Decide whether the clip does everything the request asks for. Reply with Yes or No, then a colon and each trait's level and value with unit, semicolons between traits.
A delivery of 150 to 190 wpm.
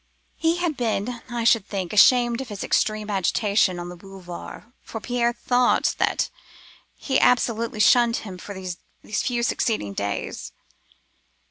No: average, 140 wpm